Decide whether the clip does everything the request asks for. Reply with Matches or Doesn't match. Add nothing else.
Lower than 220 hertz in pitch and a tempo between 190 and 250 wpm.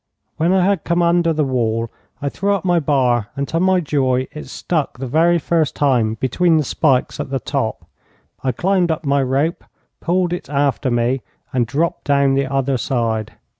Matches